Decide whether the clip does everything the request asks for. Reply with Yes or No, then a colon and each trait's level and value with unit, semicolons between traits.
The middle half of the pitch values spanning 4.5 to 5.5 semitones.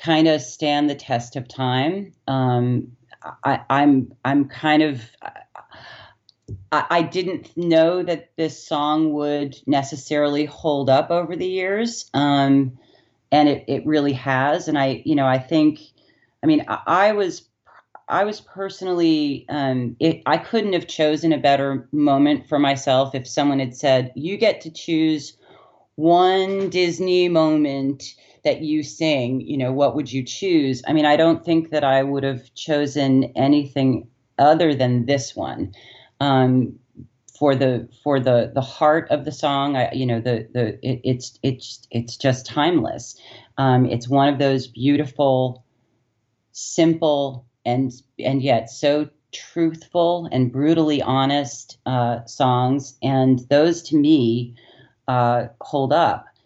No: average, 3.3 semitones